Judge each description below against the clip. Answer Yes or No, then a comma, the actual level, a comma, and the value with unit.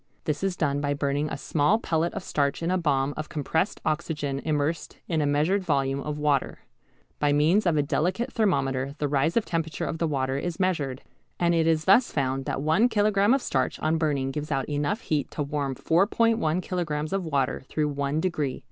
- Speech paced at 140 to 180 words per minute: No, average, 200 wpm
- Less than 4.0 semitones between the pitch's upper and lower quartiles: Yes, average, 3.4 semitones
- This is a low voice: No, medium, 155 Hz